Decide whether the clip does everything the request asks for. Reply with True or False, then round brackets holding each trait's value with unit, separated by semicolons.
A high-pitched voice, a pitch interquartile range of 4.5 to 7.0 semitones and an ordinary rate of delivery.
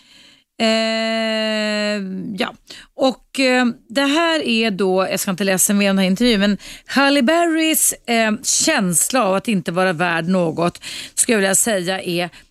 True (215 Hz; 5.2 semitones; 155 wpm)